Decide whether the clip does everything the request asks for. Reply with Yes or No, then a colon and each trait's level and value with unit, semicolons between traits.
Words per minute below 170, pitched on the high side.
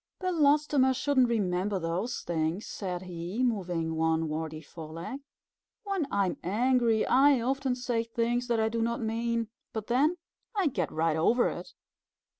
Yes: average, 150 wpm; high, 230 Hz